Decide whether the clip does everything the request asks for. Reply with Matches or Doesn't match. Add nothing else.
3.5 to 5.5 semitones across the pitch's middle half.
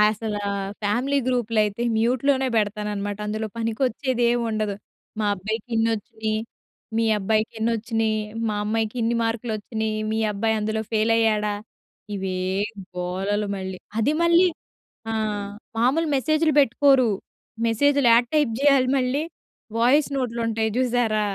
Doesn't match